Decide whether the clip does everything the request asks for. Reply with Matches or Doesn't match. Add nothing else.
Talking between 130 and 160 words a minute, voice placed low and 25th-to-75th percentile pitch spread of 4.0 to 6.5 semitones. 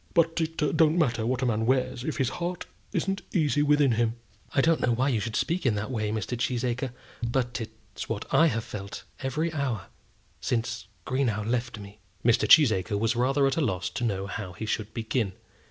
Doesn't match